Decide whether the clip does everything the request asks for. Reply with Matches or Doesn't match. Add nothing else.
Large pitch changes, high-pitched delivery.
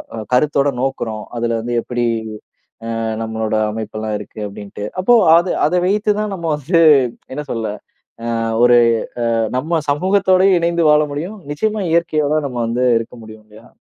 Doesn't match